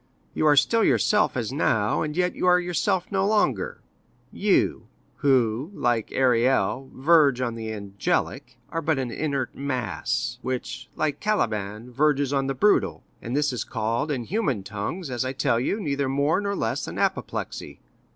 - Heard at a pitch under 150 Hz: Yes, low, 135 Hz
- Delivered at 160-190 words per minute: Yes, average, 165 wpm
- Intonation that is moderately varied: Yes, average, 4.8 semitones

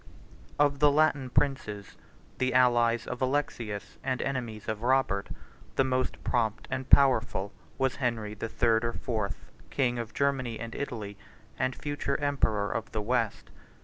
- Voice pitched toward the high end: No, low, 125 Hz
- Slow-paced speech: No, average, 150 wpm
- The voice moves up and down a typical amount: Yes, average, 3.4 semitones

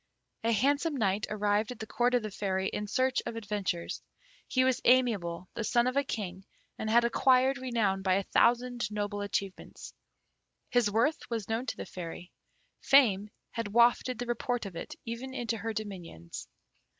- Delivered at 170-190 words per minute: Yes, average, 175 wpm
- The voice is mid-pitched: No, high, 225 Hz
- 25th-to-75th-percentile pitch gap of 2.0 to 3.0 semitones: No, average, 3.4 semitones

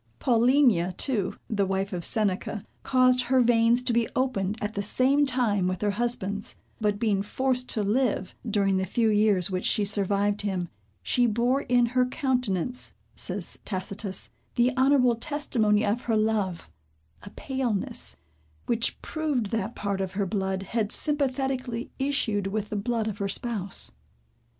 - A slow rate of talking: No, average, 155 wpm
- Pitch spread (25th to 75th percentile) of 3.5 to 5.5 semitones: Yes, average, 3.9 semitones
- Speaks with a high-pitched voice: Yes, high, 220 Hz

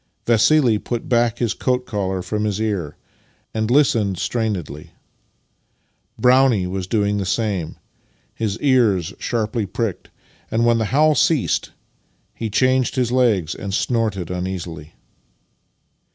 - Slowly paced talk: Yes, slow, 125 wpm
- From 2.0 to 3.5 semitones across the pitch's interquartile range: No, average, 4.2 semitones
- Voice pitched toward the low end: Yes, low, 110 Hz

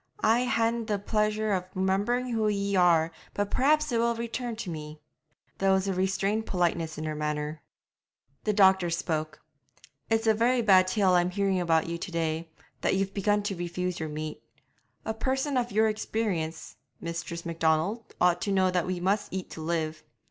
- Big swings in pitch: No, average, 4.5 semitones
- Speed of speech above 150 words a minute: Yes, average, 175 wpm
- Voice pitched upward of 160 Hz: Yes, high, 190 Hz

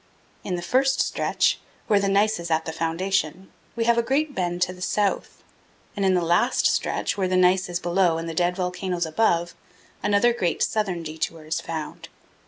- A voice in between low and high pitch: Yes, medium, 180 Hz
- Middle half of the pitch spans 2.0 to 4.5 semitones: Yes, average, 3.0 semitones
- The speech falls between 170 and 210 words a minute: Yes, average, 190 wpm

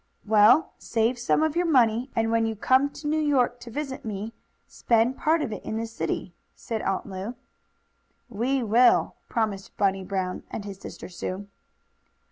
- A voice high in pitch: Yes, high, 225 Hz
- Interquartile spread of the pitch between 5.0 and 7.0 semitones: No, average, 4.1 semitones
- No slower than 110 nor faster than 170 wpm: No, average, 180 wpm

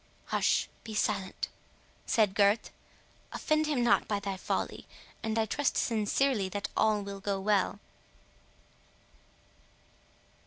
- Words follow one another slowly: Yes, slow, 110 wpm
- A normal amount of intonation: No, narrow, 2.3 semitones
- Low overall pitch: No, high, 210 Hz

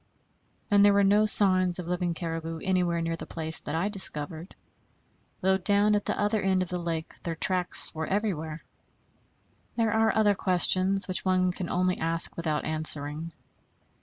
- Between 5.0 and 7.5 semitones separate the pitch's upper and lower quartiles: No, average, 3.1 semitones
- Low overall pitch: No, medium, 180 Hz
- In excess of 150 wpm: Yes, average, 165 wpm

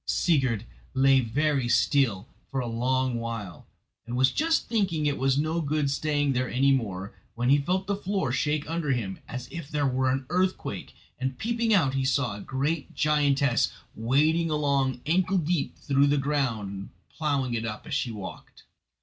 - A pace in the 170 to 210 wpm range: Yes, average, 175 wpm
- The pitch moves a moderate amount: Yes, average, 3.6 semitones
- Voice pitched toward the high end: No, medium, 140 Hz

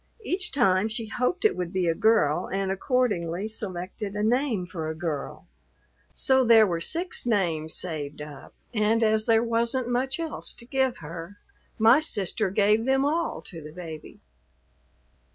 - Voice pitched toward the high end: Yes, high, 210 Hz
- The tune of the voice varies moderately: No, wide, 5.9 semitones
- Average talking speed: Yes, average, 160 wpm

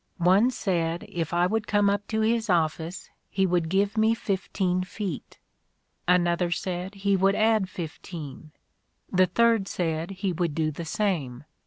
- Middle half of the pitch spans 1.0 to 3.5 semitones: Yes, average, 3.1 semitones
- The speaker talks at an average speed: Yes, average, 155 wpm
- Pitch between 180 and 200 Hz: Yes, medium, 185 Hz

